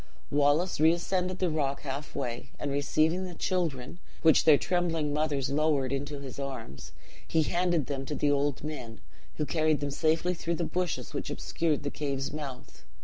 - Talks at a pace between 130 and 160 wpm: No, average, 170 wpm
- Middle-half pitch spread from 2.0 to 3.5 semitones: Yes, average, 2.9 semitones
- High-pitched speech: No, medium, 150 Hz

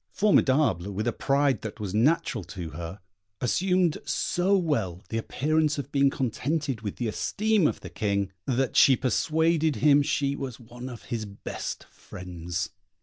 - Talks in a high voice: No, low, 130 Hz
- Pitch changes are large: Yes, wide, 6.5 semitones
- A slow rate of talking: No, average, 155 wpm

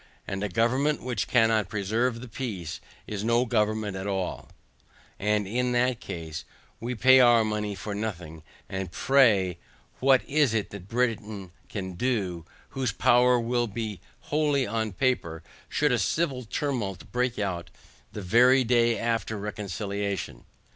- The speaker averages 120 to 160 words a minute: Yes, average, 145 wpm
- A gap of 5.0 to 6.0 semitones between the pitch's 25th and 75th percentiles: No, average, 3.9 semitones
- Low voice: Yes, low, 110 Hz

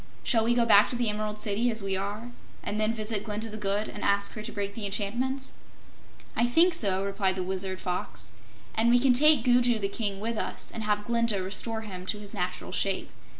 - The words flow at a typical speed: No, fast, 220 wpm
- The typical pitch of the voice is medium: No, high, 215 Hz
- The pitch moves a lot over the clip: No, average, 2.8 semitones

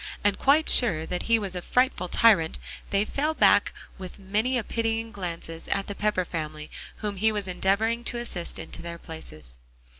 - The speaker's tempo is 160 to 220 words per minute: Yes, average, 180 wpm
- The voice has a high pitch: Yes, high, 200 Hz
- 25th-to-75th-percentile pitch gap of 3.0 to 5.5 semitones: Yes, average, 4.7 semitones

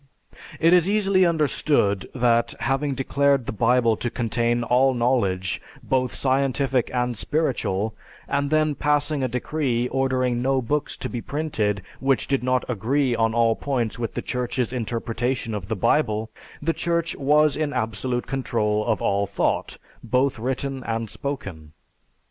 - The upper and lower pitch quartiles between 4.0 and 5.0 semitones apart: No, average, 3.6 semitones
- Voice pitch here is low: Yes, low, 125 Hz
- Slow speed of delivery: No, average, 150 wpm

